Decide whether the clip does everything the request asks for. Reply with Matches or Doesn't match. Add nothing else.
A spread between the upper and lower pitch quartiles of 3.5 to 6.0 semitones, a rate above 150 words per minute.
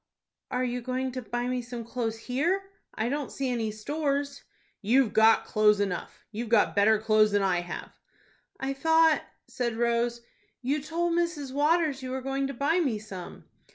Matches